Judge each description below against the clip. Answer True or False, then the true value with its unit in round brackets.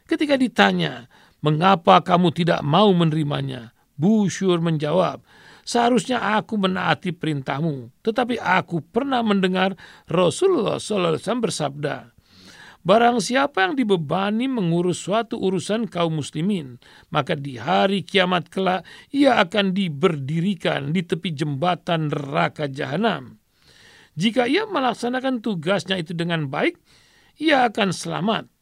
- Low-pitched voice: False (185 Hz)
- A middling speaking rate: True (110 wpm)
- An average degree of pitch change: False (5.8 semitones)